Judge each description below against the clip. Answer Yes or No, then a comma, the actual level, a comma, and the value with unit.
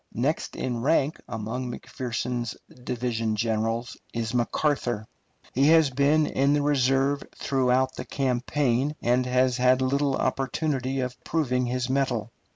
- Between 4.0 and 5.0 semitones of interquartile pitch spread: No, narrow, 2.4 semitones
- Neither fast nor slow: No, slow, 130 wpm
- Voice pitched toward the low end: Yes, low, 130 Hz